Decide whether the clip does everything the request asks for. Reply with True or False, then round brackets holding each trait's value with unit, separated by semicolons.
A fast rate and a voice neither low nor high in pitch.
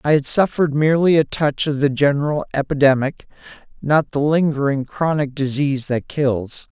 False (150 wpm; 145 Hz)